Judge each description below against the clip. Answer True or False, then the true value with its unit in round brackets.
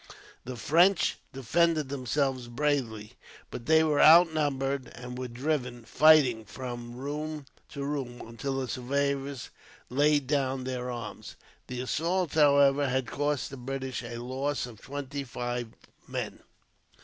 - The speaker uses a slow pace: True (130 wpm)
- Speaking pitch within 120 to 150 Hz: True (135 Hz)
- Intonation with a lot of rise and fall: False (2.9 semitones)